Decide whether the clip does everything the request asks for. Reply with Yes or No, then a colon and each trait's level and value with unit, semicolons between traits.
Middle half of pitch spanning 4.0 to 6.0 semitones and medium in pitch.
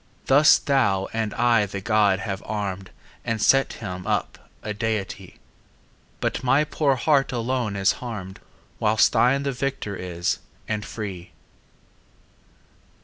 No: average, 4.5 semitones; low, 110 Hz